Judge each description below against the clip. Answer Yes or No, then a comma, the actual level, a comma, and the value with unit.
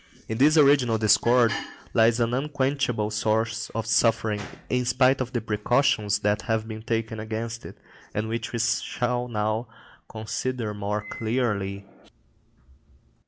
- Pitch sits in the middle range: No, low, 115 Hz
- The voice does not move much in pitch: Yes, narrow, 2.3 semitones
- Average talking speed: No, slow, 130 wpm